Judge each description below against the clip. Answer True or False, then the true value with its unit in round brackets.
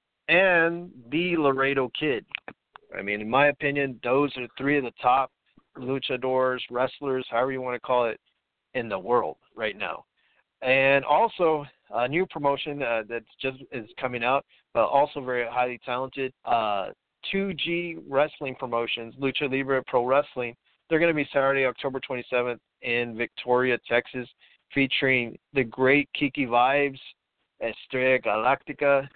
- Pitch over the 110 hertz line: True (135 Hz)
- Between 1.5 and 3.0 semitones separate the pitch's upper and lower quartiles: True (2.7 semitones)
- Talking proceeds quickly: False (140 wpm)